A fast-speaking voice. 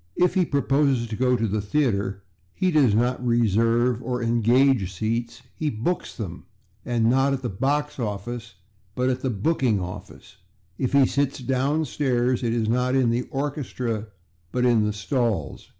No: average, 165 wpm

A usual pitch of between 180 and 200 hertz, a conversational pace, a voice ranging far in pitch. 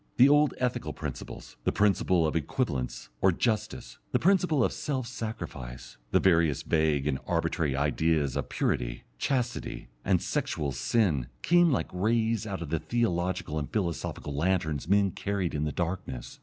No: very low, 85 Hz; average, 155 wpm; wide, 7.5 semitones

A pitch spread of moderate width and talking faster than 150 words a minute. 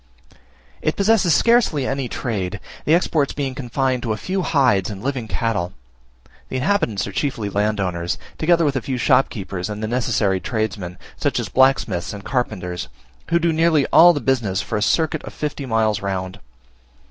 No: wide, 6.4 semitones; average, 170 wpm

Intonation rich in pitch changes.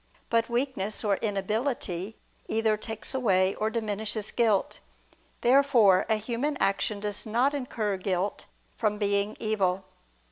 No: average, 2.7 semitones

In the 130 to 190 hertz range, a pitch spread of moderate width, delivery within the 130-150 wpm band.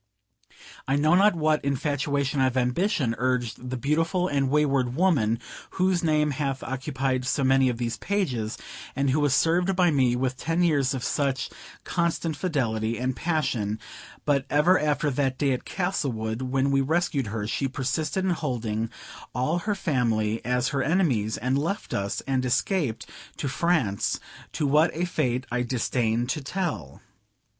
No: low, 135 Hz; average, 4.0 semitones; average, 160 wpm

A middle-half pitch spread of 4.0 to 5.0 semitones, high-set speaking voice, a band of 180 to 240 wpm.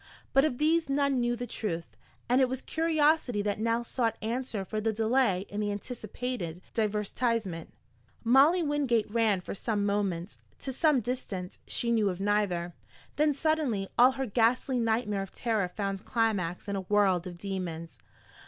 No: average, 4.4 semitones; high, 225 Hz; average, 160 wpm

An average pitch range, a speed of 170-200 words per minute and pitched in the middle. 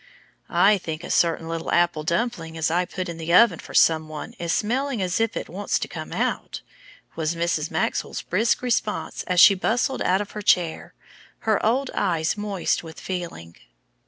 Yes: average, 4.3 semitones; average, 185 wpm; medium, 180 Hz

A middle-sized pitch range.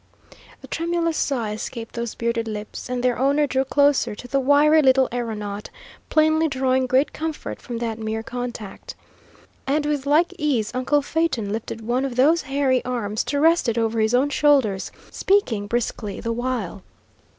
Yes: average, 4.2 semitones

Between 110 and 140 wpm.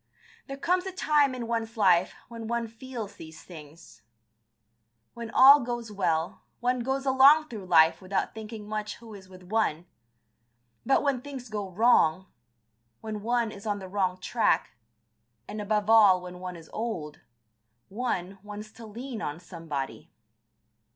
No: average, 150 wpm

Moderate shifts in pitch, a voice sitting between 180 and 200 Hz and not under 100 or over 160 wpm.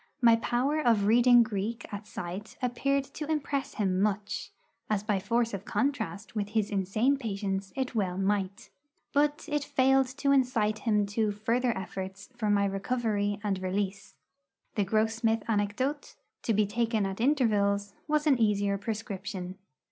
No: average, 3.7 semitones; high, 215 Hz; average, 150 wpm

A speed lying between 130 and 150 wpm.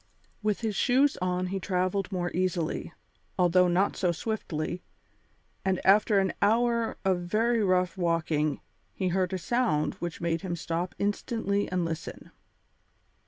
Yes: average, 140 wpm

